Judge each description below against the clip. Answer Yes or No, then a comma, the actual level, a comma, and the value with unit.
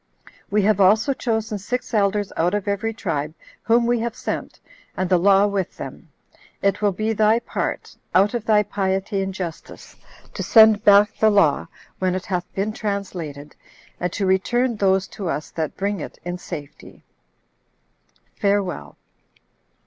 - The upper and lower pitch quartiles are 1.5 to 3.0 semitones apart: Yes, narrow, 2.6 semitones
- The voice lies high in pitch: Yes, high, 200 Hz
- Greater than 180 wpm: No, average, 155 wpm